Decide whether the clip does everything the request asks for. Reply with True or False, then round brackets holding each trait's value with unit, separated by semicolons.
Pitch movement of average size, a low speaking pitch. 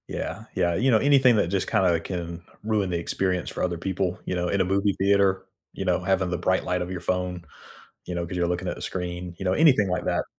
False (1.8 semitones; 90 Hz)